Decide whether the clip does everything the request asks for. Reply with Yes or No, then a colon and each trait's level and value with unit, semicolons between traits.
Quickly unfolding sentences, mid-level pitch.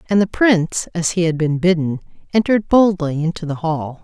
No: average, 195 wpm; medium, 170 Hz